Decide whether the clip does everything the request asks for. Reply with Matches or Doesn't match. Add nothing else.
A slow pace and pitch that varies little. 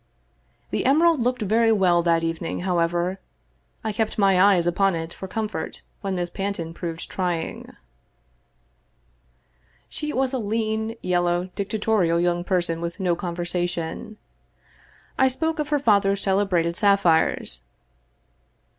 Doesn't match